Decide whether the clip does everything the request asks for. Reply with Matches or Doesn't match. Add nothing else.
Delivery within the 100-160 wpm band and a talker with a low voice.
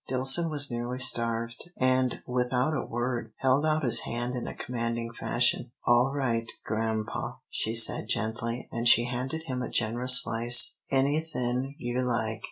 Matches